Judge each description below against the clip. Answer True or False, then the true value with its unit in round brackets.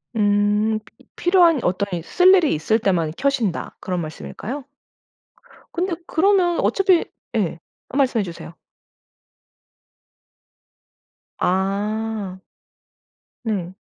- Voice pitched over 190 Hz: True (215 Hz)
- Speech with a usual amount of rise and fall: False (8.0 semitones)